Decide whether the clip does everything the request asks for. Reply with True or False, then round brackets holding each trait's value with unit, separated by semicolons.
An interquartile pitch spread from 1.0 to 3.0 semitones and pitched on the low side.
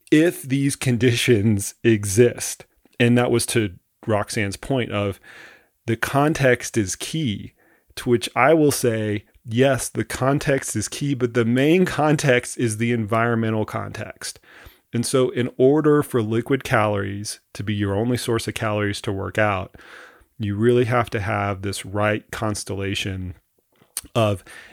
False (3.4 semitones; 115 Hz)